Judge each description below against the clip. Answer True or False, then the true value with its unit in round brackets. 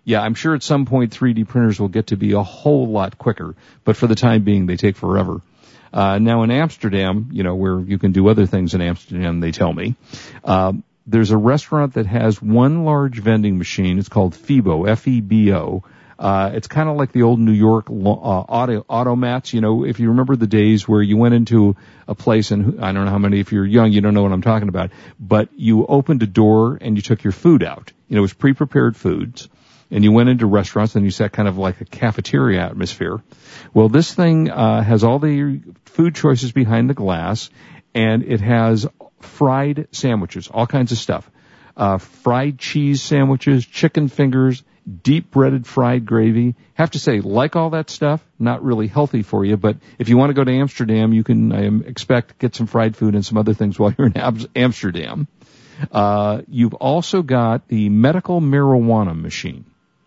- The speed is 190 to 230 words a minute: True (200 wpm)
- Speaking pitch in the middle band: False (115 Hz)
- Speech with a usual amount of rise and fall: True (4.2 semitones)